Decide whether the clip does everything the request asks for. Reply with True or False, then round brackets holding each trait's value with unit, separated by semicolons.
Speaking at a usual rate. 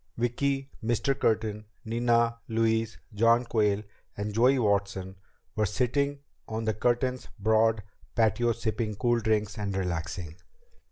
False (125 wpm)